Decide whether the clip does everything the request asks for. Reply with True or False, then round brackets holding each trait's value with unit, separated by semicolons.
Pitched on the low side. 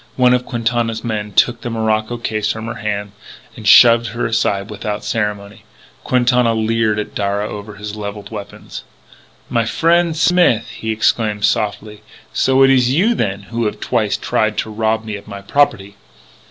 True (110 Hz)